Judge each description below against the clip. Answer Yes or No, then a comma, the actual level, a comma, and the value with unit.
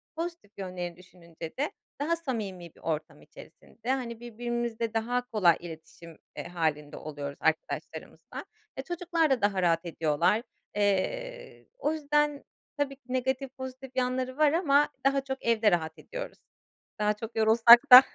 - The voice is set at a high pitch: Yes, high, 235 Hz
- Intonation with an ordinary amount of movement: No, wide, 7.5 semitones